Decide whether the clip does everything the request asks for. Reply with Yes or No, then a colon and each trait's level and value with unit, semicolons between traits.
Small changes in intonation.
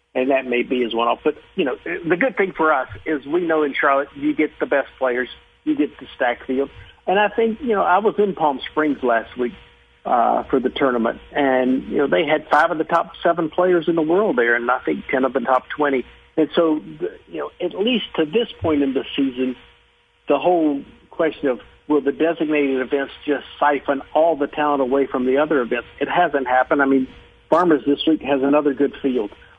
No: average, 3.8 semitones